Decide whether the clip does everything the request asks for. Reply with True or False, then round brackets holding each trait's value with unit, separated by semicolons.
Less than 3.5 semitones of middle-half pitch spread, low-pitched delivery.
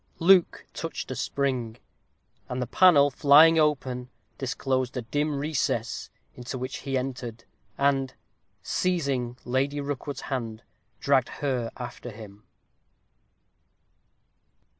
True (2.7 semitones; 130 Hz)